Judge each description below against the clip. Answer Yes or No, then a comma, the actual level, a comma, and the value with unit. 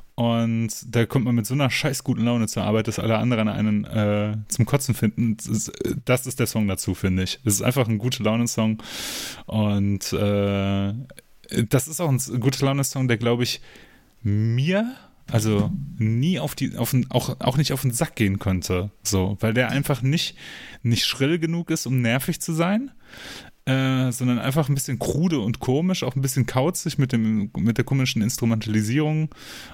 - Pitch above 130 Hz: No, low, 120 Hz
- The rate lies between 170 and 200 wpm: Yes, fast, 190 wpm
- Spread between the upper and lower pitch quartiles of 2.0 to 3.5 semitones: No, average, 3.9 semitones